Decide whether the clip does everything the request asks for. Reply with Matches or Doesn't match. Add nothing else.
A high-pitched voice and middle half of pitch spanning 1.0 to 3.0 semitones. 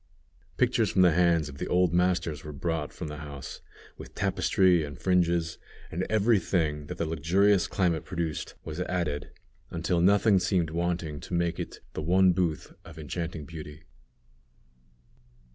Doesn't match